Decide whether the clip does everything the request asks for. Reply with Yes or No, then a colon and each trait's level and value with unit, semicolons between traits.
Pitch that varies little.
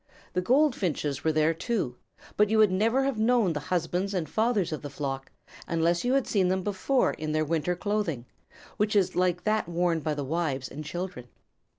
No: average, 5.3 semitones